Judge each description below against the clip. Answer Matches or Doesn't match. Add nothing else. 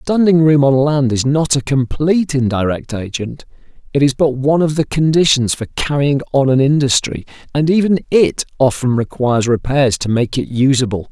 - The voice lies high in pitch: Doesn't match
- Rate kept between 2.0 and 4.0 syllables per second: Doesn't match